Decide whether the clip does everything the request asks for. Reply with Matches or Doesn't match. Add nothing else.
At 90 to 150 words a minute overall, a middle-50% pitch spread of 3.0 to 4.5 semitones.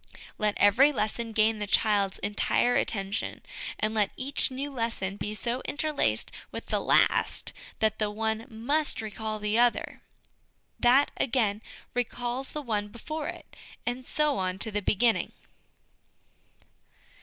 Matches